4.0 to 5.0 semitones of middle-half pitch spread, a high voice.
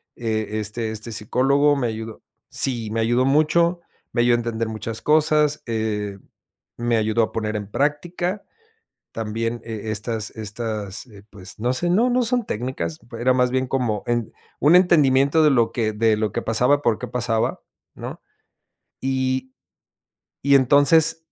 No: average, 4.3 semitones; low, 120 Hz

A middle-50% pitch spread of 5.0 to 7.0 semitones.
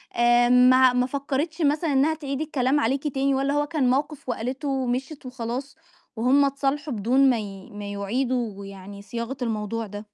No: average, 3.3 semitones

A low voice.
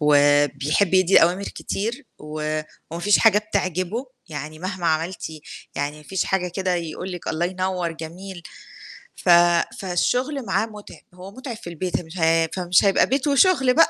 No: medium, 180 Hz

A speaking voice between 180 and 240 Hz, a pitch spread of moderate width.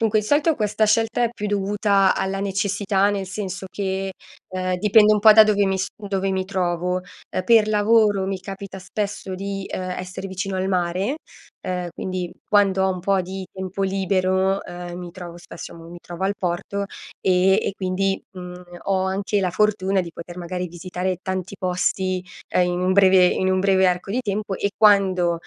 No: high, 190 Hz; narrow, 1.6 semitones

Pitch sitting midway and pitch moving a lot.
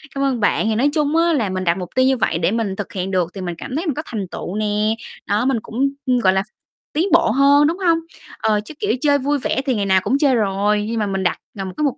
No: high, 225 Hz; wide, 6.4 semitones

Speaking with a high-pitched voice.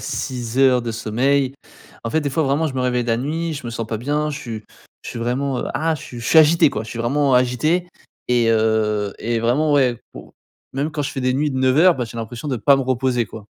No: low, 130 Hz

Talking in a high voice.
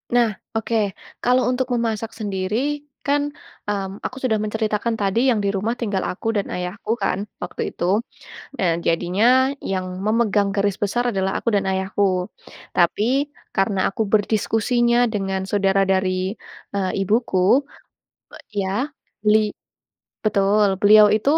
Yes: high, 205 Hz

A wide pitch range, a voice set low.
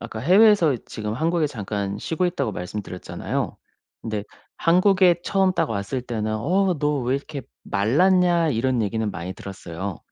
Yes: wide, 8.7 semitones; low, 130 Hz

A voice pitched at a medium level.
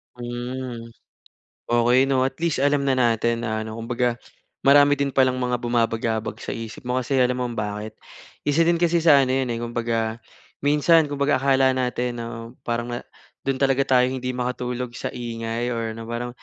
No: low, 125 Hz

